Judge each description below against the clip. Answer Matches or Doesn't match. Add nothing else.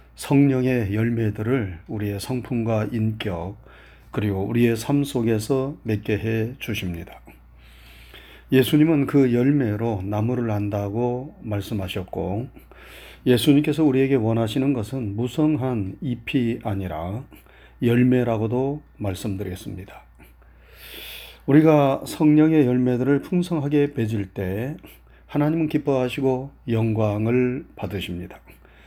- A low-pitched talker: Matches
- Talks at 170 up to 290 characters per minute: Matches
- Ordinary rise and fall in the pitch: Matches